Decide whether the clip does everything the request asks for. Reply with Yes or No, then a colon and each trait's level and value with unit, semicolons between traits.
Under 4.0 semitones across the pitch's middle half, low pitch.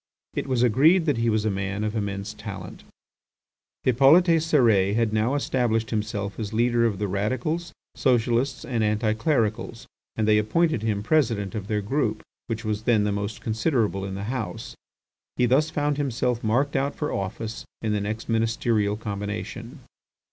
Yes: average, 3.6 semitones; low, 110 Hz